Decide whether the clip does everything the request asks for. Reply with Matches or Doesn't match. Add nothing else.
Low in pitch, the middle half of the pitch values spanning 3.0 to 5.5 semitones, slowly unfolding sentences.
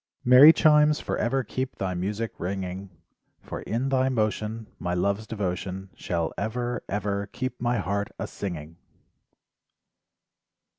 Matches